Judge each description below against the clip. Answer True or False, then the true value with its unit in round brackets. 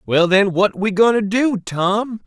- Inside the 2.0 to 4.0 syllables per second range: True (3.9 syllables/s)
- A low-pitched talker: False (205 Hz)